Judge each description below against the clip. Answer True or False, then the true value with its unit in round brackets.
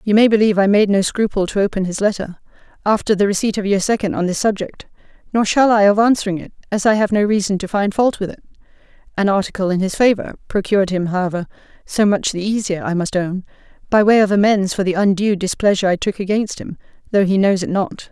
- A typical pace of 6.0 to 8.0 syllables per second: True (6.3 syllables/s)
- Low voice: False (200 Hz)